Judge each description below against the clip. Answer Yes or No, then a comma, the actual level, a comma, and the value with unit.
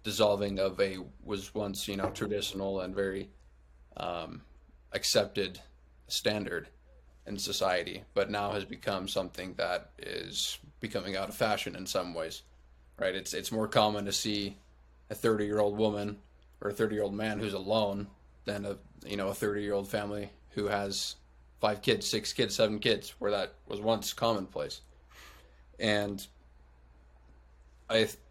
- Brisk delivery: No, average, 155 wpm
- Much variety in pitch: Yes, wide, 8.3 semitones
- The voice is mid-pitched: No, low, 100 Hz